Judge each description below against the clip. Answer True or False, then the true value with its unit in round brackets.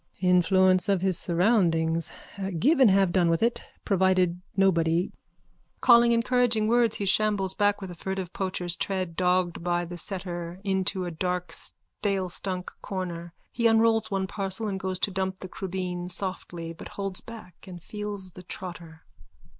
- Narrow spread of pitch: True (2.3 semitones)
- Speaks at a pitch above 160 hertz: True (185 Hz)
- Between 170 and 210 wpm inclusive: False (155 wpm)